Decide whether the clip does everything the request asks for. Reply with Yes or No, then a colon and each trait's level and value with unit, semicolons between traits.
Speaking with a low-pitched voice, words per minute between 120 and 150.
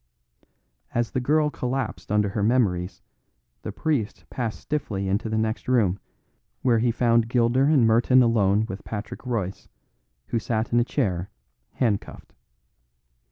Yes: low, 115 Hz; average, 140 wpm